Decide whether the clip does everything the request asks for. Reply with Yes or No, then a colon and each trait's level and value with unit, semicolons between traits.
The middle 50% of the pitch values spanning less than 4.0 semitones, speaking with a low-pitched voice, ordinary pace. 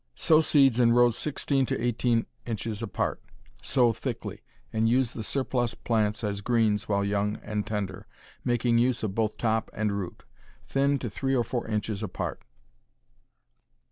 Yes: average, 2.7 semitones; low, 115 Hz; average, 155 wpm